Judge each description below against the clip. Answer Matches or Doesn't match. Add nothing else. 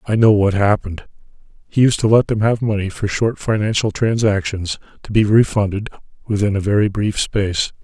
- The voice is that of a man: Matches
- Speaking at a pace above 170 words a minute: Doesn't match